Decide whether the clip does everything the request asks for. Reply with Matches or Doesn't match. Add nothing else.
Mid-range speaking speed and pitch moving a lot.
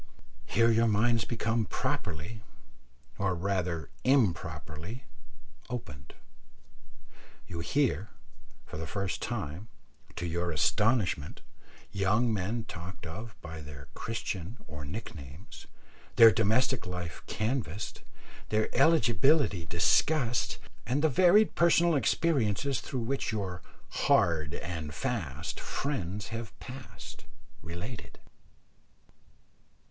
Doesn't match